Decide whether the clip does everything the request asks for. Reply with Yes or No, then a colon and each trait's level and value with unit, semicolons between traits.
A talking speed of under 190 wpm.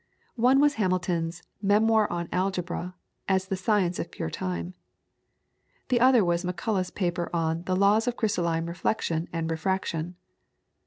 Yes: average, 140 wpm